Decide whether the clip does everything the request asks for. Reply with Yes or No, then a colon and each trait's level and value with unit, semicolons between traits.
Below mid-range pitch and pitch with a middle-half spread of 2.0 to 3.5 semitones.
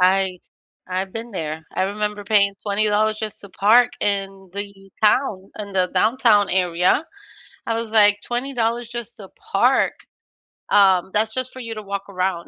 No: high, 205 Hz; narrow, 2.5 semitones